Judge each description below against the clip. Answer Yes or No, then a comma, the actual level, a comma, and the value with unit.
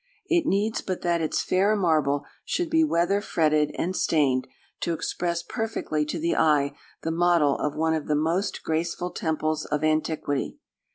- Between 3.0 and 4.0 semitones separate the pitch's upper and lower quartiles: Yes, average, 3.3 semitones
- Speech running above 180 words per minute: No, average, 165 wpm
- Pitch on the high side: No, medium, 165 Hz